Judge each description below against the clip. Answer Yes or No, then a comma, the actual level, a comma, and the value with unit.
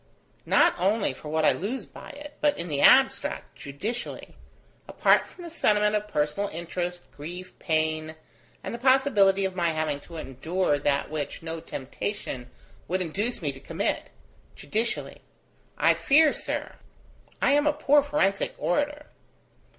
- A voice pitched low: No, medium, 185 Hz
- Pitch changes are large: Yes, wide, 7.3 semitones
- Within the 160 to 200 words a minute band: No, average, 150 wpm